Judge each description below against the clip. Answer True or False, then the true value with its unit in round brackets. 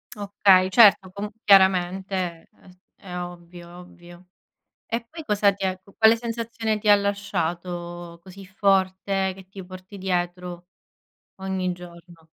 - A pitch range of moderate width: False (2.2 semitones)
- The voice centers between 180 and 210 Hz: True (190 Hz)